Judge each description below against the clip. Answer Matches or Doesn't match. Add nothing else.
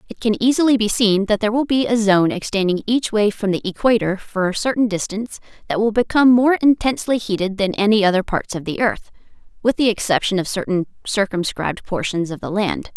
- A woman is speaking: Matches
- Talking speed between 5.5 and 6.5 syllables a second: Matches